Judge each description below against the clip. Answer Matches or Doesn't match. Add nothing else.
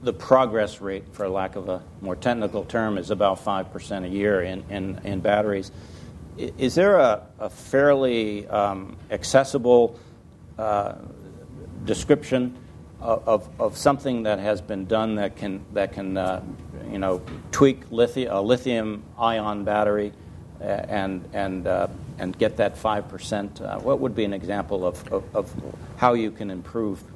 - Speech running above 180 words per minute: Doesn't match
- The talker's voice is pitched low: Matches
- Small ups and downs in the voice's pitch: Doesn't match